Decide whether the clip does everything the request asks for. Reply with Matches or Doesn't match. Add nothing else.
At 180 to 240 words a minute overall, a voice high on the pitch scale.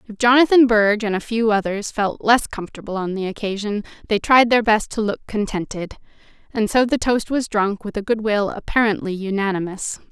Matches